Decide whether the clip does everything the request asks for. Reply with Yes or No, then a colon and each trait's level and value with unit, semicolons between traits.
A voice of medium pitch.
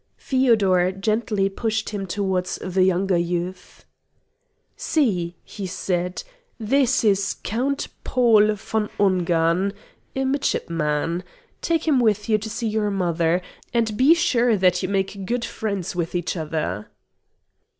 No: high, 195 Hz